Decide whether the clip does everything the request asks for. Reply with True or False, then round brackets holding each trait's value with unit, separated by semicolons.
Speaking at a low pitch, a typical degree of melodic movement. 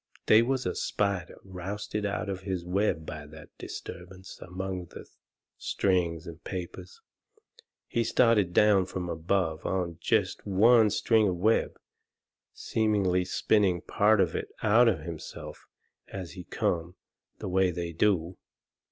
True (95 Hz; 3.1 semitones)